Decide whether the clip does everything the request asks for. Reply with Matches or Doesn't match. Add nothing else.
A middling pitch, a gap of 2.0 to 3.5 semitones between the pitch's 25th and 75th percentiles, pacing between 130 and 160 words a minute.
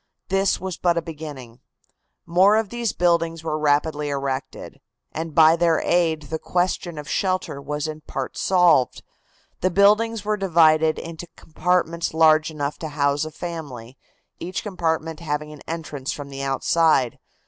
Matches